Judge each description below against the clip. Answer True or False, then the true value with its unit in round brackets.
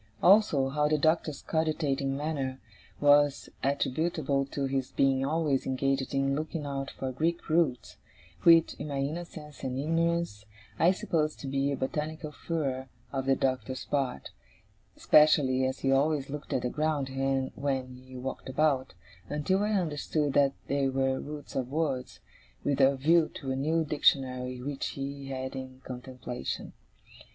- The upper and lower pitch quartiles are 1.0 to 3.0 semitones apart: True (2.6 semitones)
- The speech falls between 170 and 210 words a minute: False (150 wpm)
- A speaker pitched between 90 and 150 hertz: True (140 Hz)